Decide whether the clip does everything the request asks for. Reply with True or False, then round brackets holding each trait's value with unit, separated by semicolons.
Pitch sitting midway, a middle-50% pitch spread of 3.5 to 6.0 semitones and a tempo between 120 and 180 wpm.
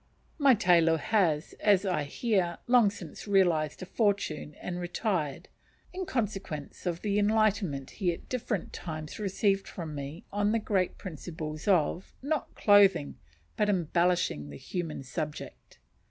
True (180 Hz; 4.8 semitones; 140 wpm)